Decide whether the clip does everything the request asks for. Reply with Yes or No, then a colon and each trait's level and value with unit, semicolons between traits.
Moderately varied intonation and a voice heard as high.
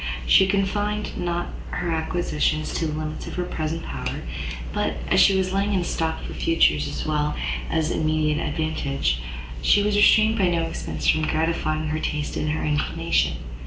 No: average, 3.1 semitones; medium, 160 Hz